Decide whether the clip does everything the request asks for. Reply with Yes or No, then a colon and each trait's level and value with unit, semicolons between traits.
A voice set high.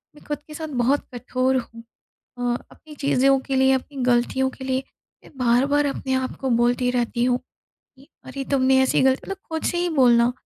Yes: very high, 265 Hz